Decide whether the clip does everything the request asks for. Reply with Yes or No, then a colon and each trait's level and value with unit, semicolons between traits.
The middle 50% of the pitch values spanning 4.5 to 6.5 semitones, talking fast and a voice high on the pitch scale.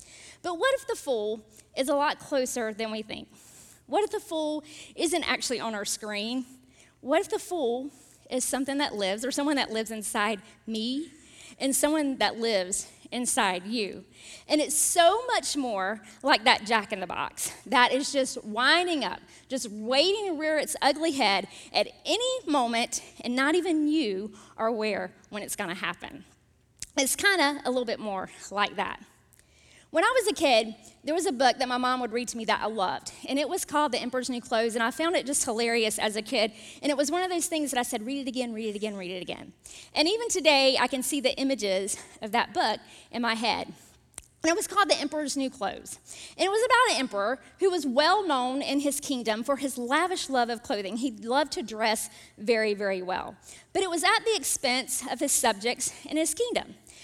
Yes: average, 5.2 semitones; fast, 210 wpm; very high, 265 Hz